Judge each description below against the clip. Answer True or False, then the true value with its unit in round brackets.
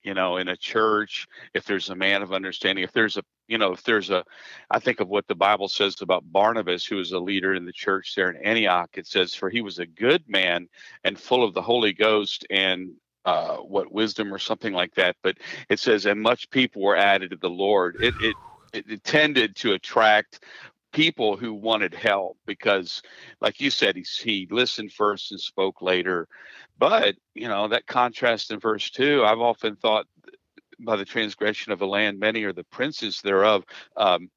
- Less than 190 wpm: False (200 wpm)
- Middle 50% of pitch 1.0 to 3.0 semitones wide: True (2.5 semitones)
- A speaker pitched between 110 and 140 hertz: False (100 Hz)